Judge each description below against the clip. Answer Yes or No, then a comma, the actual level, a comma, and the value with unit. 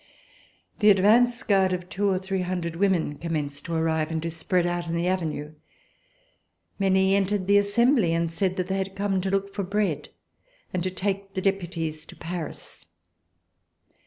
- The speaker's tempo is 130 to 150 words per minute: No, average, 170 wpm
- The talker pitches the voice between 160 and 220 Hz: Yes, medium, 185 Hz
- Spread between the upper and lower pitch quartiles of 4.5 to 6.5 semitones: No, average, 2.8 semitones